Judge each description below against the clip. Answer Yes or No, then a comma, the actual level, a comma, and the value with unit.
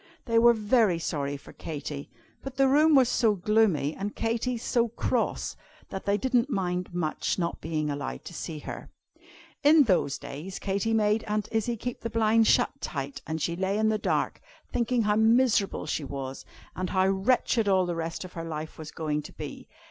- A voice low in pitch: No, high, 200 Hz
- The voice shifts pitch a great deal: Yes, wide, 5.8 semitones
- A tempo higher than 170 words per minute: Yes, average, 190 wpm